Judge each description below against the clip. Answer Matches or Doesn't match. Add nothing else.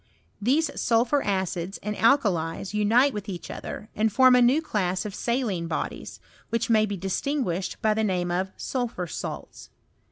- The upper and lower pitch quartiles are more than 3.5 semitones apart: Matches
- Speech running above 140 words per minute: Matches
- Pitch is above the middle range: Matches